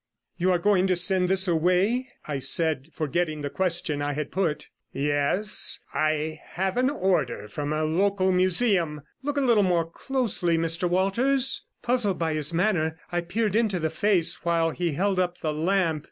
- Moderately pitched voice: Yes, medium, 175 Hz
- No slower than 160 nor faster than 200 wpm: Yes, average, 170 wpm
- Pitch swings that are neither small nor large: Yes, average, 3.8 semitones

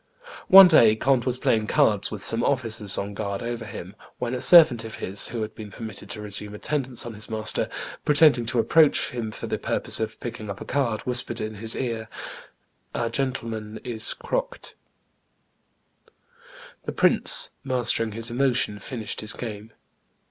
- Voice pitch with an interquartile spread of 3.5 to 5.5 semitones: No, average, 2.8 semitones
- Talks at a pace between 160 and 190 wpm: Yes, average, 165 wpm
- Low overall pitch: Yes, low, 115 Hz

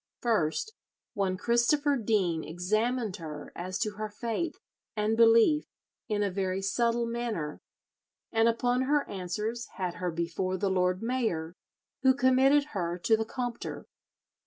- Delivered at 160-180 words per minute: No, slow, 135 wpm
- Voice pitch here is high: Yes, high, 215 Hz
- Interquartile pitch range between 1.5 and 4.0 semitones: No, average, 4.6 semitones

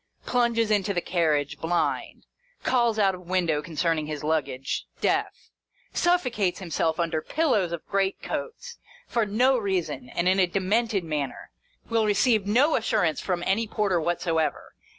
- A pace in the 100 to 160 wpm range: Yes, average, 145 wpm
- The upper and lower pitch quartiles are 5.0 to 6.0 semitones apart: Yes, wide, 5.4 semitones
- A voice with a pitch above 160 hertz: Yes, high, 190 Hz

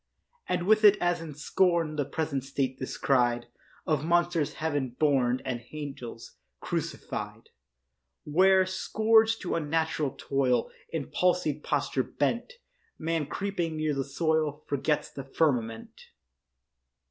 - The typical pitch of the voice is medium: Yes, medium, 155 Hz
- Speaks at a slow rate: Yes, slow, 120 wpm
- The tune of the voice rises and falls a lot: No, average, 4.1 semitones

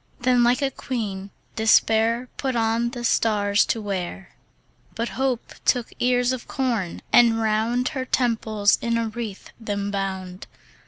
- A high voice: Yes, high, 230 Hz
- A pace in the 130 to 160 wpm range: Yes, average, 145 wpm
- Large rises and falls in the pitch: No, average, 3.1 semitones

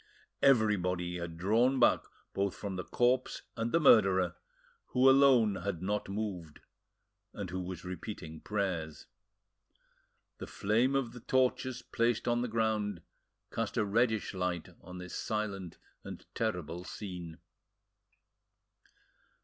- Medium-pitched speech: No, low, 100 Hz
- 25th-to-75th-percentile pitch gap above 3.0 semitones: Yes, average, 4.5 semitones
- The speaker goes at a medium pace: No, slow, 125 wpm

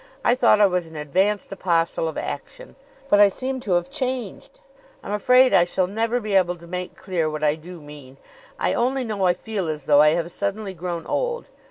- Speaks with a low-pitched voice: No, medium, 185 Hz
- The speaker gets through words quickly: Yes, fast, 210 wpm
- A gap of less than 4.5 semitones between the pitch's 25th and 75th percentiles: No, average, 5.0 semitones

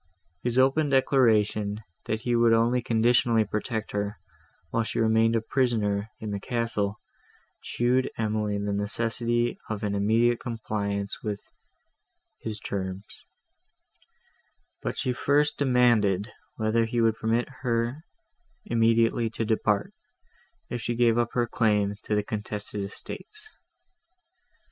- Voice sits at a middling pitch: No, low, 115 Hz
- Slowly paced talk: Yes, slow, 125 wpm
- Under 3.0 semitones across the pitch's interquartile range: Yes, narrow, 2.4 semitones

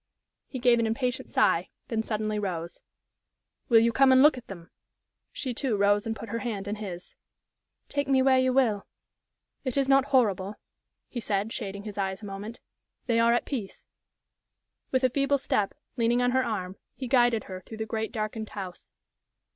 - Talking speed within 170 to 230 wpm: Yes, average, 185 wpm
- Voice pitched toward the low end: No, high, 225 Hz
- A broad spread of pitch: No, average, 4.1 semitones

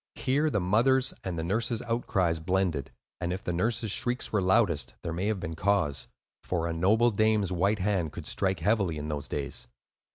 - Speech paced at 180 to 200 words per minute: Yes, average, 190 wpm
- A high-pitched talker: No, very low, 95 Hz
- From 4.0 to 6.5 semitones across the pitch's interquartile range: Yes, average, 4.6 semitones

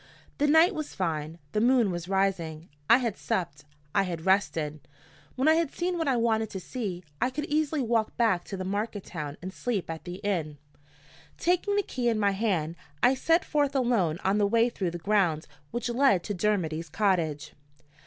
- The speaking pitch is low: No, high, 205 Hz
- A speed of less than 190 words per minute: No, average, 195 wpm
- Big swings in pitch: Yes, wide, 6.3 semitones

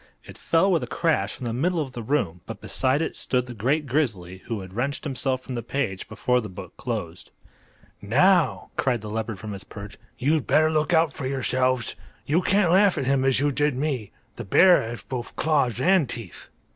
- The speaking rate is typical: No, fast, 210 wpm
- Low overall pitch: Yes, low, 130 Hz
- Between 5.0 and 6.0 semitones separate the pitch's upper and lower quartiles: Yes, average, 5.3 semitones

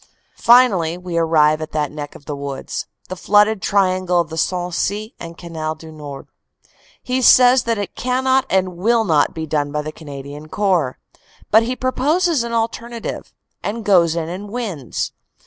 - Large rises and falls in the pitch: Yes, wide, 6.6 semitones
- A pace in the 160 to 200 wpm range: Yes, average, 165 wpm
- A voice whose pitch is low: No, medium, 180 Hz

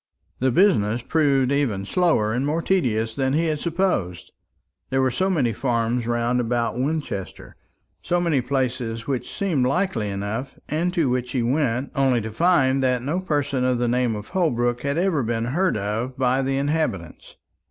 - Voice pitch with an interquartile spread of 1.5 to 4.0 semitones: No, average, 4.5 semitones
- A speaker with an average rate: Yes, average, 175 wpm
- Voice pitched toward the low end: Yes, low, 130 Hz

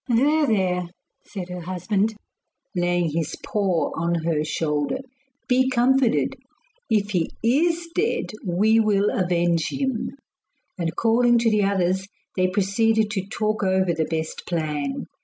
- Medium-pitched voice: No, high, 195 Hz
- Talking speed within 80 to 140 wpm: Yes, slow, 135 wpm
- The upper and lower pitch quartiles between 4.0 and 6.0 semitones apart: Yes, average, 4.7 semitones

